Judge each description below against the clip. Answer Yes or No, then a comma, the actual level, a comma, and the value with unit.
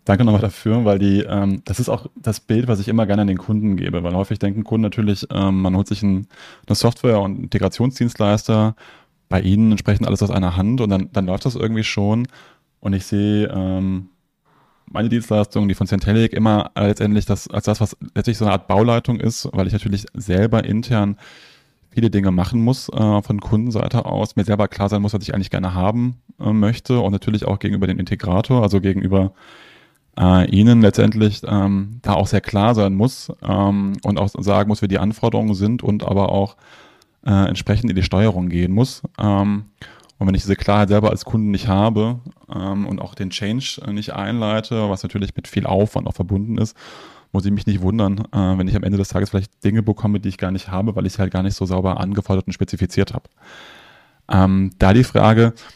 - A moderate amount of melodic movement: No, narrow, 2.2 semitones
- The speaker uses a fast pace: Yes, fast, 205 wpm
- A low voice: Yes, low, 105 Hz